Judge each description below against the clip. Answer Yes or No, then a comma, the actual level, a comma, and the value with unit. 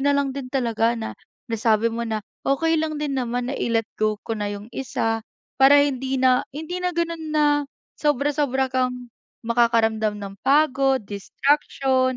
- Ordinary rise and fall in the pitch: Yes, average, 3.8 semitones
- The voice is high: Yes, very high, 255 Hz